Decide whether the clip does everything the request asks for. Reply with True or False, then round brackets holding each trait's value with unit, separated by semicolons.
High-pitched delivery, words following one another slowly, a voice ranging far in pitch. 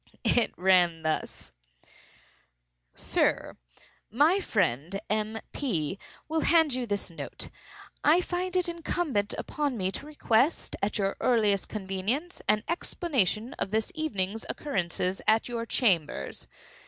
True (220 Hz; 115 wpm; 7.7 semitones)